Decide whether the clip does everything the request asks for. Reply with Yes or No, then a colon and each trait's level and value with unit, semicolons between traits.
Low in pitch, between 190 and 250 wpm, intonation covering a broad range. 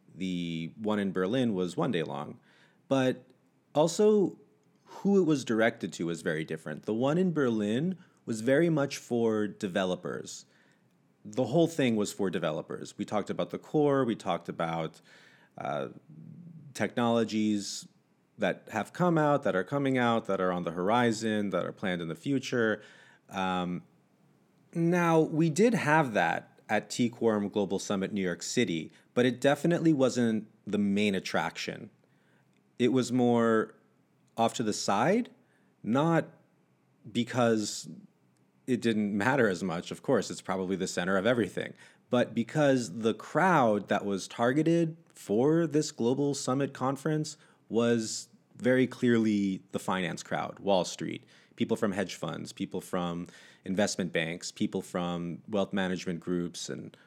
No: low, 115 Hz; average, 145 wpm; wide, 6.5 semitones